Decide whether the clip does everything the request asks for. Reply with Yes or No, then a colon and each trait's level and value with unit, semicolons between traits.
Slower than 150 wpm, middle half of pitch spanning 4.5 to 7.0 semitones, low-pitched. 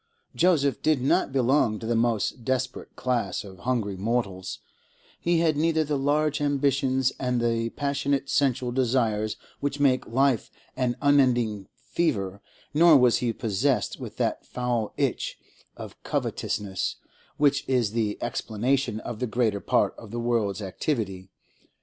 No: average, 140 wpm; average, 4.1 semitones; low, 125 Hz